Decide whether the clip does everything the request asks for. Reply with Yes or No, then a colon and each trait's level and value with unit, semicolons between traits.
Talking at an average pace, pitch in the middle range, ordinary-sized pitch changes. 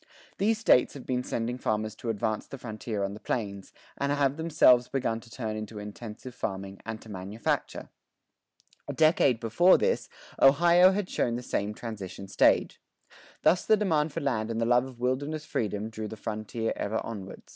No: average, 180 wpm; low, 115 Hz; average, 4.6 semitones